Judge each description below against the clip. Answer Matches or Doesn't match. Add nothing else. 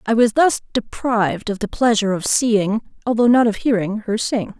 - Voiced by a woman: Matches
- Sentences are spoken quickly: Doesn't match